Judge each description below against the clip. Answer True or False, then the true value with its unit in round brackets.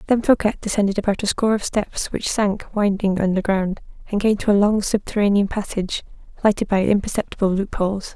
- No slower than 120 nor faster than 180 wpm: True (170 wpm)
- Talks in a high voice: True (200 Hz)